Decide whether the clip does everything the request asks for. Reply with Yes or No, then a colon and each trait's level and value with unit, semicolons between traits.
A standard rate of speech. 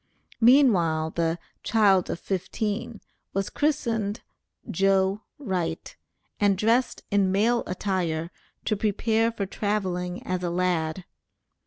No: slow, 110 wpm